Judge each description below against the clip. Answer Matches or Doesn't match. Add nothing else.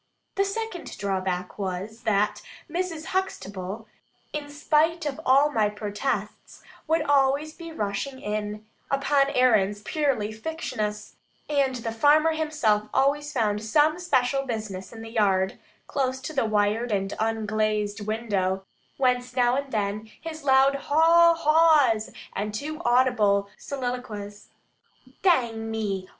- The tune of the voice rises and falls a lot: Matches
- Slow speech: Matches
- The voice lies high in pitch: Matches